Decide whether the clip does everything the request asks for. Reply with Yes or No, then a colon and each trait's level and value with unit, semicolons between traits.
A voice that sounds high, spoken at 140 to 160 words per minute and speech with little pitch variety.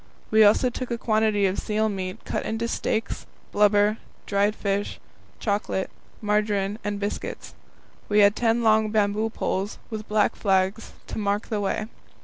Yes: high, 210 Hz; average, 150 wpm; narrow, 1.4 semitones